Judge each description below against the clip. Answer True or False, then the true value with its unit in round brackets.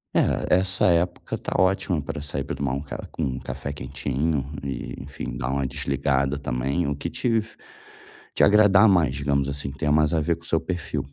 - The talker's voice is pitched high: False (70 Hz)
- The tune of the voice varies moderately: True (3.7 semitones)